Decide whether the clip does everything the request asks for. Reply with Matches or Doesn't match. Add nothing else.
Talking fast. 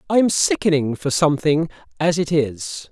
Doesn't match